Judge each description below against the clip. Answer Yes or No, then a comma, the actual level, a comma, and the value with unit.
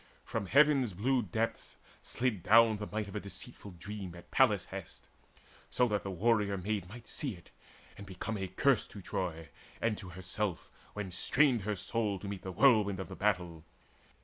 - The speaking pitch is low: Yes, low, 100 Hz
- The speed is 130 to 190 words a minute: Yes, average, 175 wpm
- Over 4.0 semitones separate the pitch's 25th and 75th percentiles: No, average, 3.5 semitones